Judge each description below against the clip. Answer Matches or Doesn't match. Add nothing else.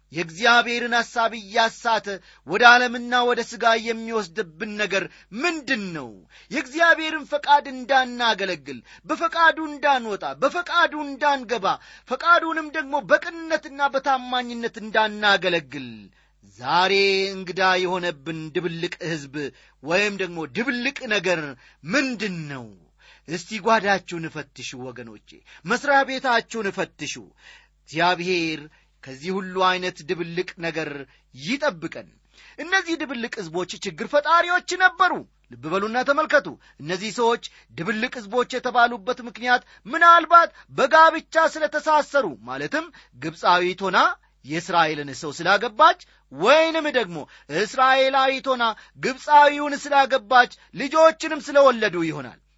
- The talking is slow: Doesn't match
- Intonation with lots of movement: Matches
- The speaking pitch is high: Matches